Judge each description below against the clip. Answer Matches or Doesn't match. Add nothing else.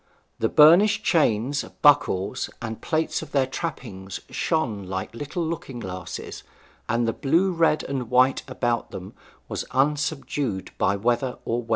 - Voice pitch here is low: Matches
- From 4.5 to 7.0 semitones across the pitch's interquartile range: Matches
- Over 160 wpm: Doesn't match